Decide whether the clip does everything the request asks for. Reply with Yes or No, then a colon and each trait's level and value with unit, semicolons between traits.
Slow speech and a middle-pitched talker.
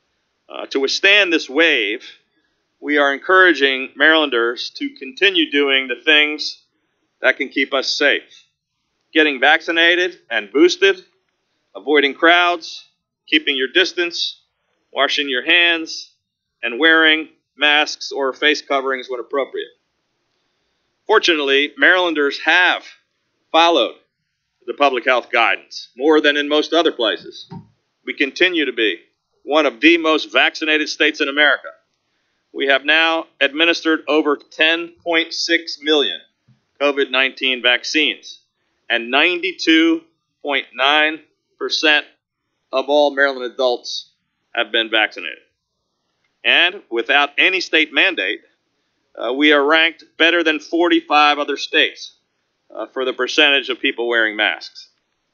Yes: slow, 115 wpm; medium, 155 Hz